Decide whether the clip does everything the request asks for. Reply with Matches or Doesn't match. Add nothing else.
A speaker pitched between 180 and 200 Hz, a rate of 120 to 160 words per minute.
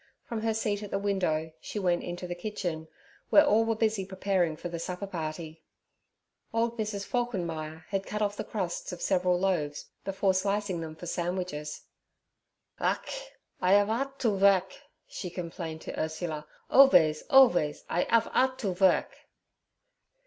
Matches